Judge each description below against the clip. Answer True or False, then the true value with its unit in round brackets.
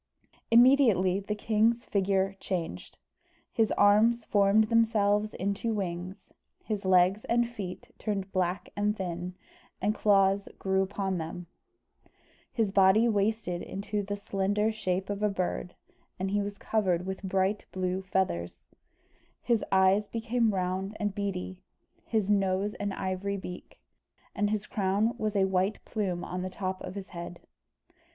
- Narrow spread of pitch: True (2.1 semitones)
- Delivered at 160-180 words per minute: False (140 wpm)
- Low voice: False (195 Hz)